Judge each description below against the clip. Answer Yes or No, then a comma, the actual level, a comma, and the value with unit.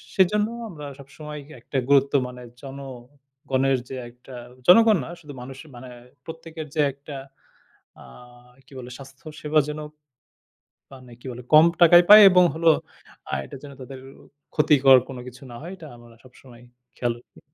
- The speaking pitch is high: No, medium, 140 Hz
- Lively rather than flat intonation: No, average, 3.3 semitones